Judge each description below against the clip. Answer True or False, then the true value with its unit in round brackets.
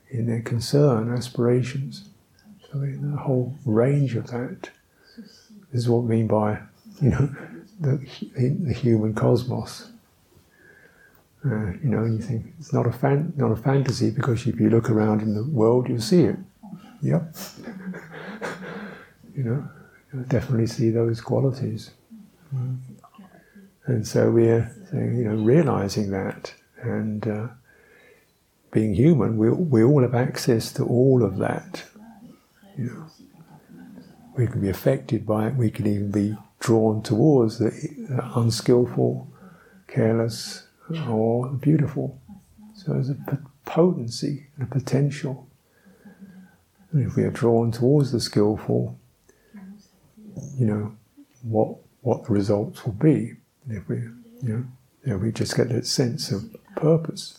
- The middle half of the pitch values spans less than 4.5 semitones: False (4.8 semitones)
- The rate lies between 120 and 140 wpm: True (135 wpm)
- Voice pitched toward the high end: False (125 Hz)